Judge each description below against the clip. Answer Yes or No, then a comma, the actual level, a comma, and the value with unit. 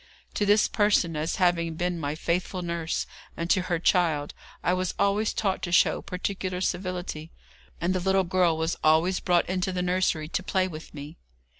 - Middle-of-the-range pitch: Yes, medium, 180 Hz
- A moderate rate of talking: Yes, average, 180 wpm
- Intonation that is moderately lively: No, narrow, 2.0 semitones